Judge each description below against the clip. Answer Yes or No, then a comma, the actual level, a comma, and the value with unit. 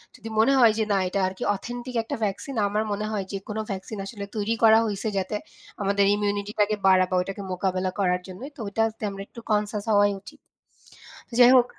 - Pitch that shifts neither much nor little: No, narrow, 2.1 semitones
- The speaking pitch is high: Yes, high, 205 Hz